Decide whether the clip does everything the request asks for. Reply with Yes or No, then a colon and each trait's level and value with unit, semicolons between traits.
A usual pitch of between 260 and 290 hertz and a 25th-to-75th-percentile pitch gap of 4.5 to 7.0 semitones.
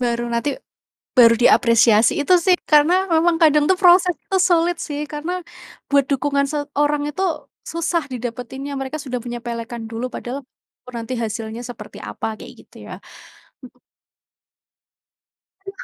Yes: very high, 280 Hz; average, 4.8 semitones